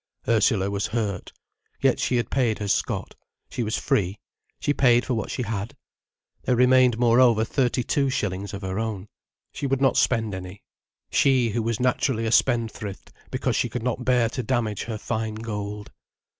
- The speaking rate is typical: Yes, average, 175 wpm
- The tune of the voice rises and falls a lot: No, average, 3.1 semitones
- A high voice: No, low, 115 Hz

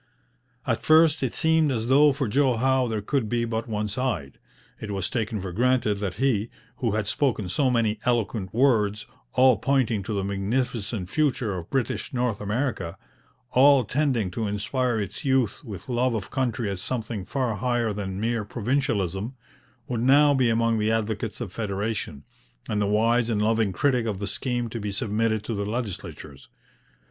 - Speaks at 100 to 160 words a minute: No, average, 175 wpm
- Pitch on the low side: Yes, low, 115 Hz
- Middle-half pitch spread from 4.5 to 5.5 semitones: No, average, 3.6 semitones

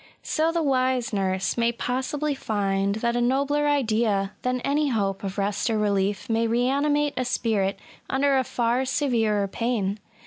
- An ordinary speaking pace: Yes, average, 160 wpm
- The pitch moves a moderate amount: Yes, average, 4.7 semitones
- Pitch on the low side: No, high, 235 Hz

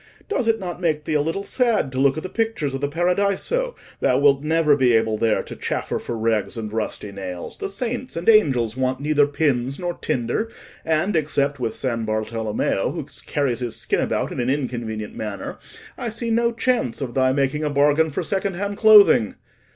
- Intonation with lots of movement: Yes, wide, 8.0 semitones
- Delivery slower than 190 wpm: No, average, 195 wpm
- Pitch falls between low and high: Yes, medium, 145 Hz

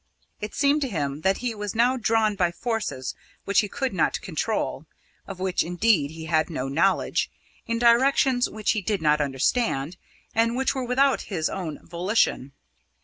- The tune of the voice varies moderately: No, wide, 6.5 semitones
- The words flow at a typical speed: Yes, average, 170 wpm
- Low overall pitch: No, high, 200 Hz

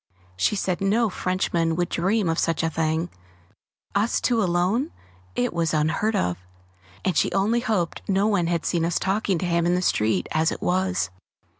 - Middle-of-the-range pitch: Yes, medium, 175 Hz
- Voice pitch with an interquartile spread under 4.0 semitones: Yes, average, 3.3 semitones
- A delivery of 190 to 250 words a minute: No, average, 180 wpm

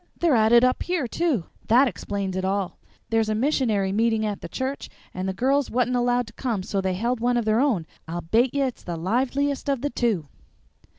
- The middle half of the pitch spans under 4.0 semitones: No, average, 4.6 semitones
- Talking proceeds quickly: Yes, fast, 225 wpm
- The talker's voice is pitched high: Yes, high, 235 Hz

